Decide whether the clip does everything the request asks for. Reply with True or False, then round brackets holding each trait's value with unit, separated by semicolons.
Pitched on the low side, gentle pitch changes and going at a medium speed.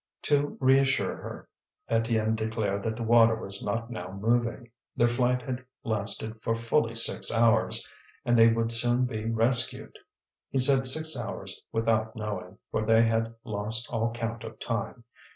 True (115 Hz; 1.5 semitones; 155 wpm)